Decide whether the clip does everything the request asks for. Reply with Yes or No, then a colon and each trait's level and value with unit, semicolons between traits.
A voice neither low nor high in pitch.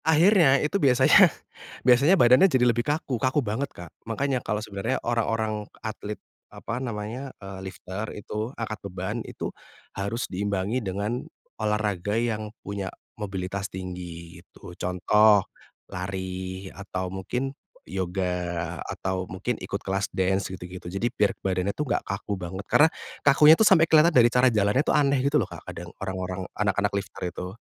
No: low, 105 Hz